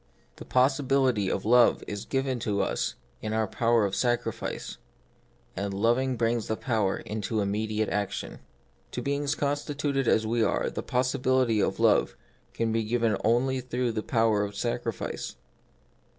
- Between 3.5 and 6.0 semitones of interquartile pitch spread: No, average, 3.1 semitones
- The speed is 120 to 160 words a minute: Yes, average, 155 wpm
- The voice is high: No, low, 115 Hz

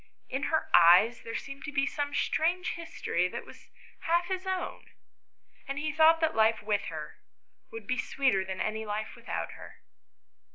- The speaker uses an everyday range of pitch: No, wide, 6.7 semitones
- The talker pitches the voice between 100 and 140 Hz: No, very high, 275 Hz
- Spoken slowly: No, average, 170 wpm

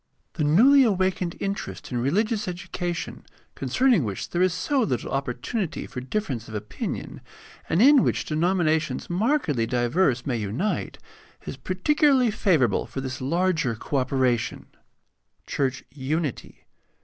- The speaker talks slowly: Yes, slow, 130 wpm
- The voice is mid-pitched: Yes, medium, 160 Hz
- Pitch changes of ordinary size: No, wide, 7.3 semitones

